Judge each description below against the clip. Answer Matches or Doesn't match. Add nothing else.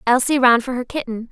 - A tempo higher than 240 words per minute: Doesn't match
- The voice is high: Matches